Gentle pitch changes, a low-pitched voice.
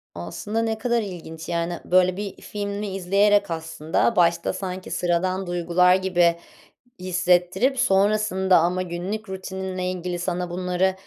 No: narrow, 2.1 semitones; medium, 185 Hz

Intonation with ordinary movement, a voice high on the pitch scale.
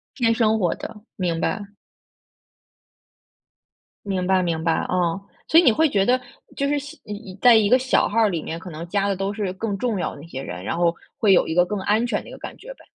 Yes: average, 4.6 semitones; high, 200 Hz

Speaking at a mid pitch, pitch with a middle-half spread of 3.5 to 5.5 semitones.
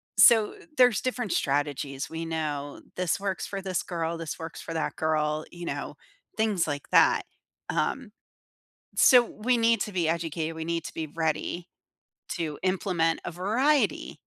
Yes: medium, 170 Hz; average, 4.7 semitones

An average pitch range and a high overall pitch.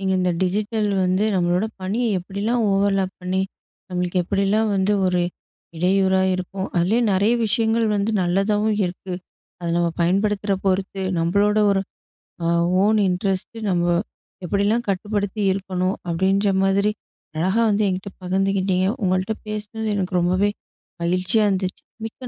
No: narrow, 2.2 semitones; high, 195 Hz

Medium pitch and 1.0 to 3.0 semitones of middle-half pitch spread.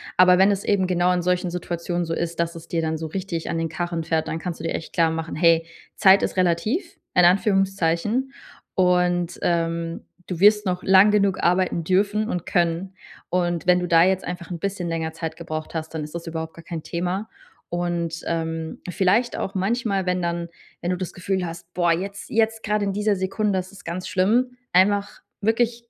Yes: medium, 180 Hz; narrow, 2.6 semitones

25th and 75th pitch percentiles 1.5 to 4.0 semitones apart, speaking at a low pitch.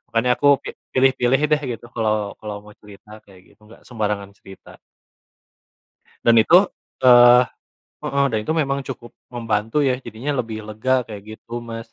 Yes: average, 3.2 semitones; low, 115 Hz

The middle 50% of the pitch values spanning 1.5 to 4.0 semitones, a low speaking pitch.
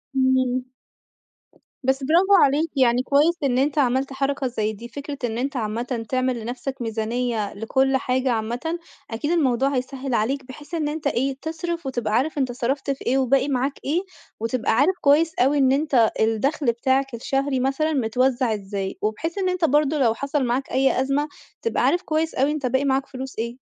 No: average, 3.0 semitones; very high, 265 Hz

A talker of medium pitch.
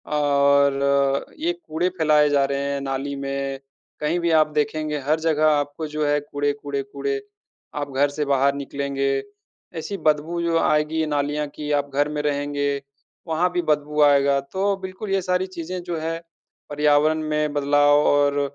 Yes: medium, 145 Hz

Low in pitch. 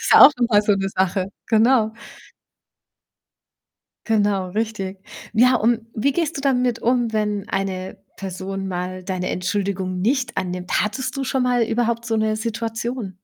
No: high, 215 Hz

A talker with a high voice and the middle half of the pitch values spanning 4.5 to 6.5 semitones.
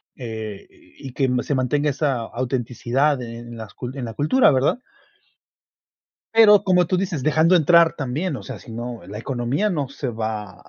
No: low, 135 Hz; average, 4.9 semitones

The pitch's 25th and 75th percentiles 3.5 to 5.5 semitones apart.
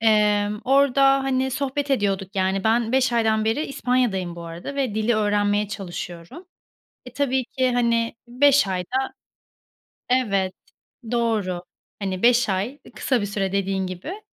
Yes: average, 4.7 semitones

